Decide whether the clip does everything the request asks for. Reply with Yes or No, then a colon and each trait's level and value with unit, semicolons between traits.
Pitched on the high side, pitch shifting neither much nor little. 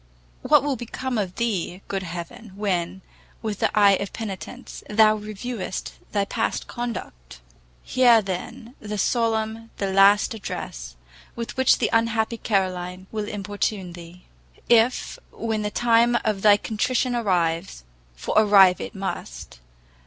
Yes: high, 210 Hz; average, 3.3 semitones